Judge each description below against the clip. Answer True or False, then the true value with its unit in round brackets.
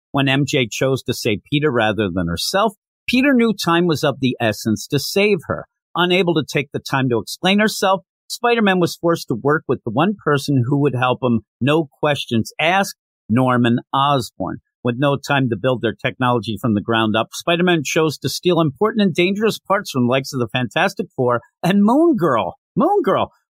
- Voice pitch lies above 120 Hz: True (140 Hz)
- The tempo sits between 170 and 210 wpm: True (195 wpm)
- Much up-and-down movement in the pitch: True (6.3 semitones)